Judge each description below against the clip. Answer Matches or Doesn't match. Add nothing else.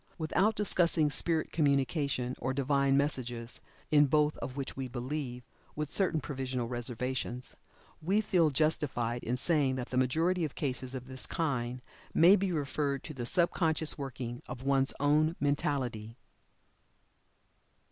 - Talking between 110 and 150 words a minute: Matches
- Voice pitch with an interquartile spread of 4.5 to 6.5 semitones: Doesn't match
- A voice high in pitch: Doesn't match